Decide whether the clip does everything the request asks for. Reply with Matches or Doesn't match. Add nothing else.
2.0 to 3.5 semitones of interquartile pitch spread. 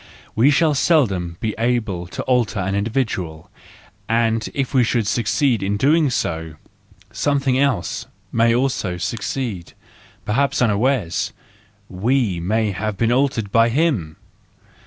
Doesn't match